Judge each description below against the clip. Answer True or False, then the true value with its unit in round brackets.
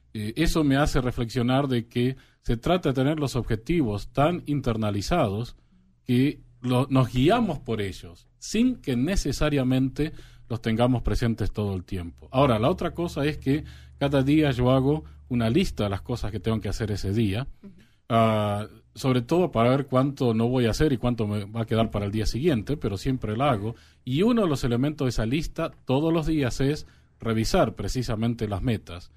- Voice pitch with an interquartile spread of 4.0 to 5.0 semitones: True (4.6 semitones)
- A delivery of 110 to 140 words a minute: False (185 wpm)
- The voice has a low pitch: True (125 Hz)